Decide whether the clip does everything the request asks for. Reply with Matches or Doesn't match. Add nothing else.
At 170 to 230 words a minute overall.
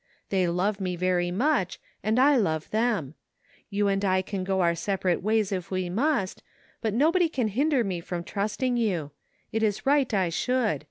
Matches